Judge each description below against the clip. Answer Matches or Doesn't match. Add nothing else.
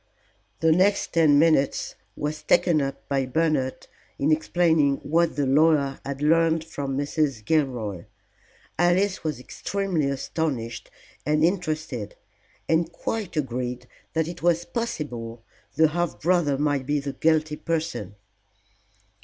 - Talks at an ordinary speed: Doesn't match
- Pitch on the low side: Doesn't match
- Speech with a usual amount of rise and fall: Matches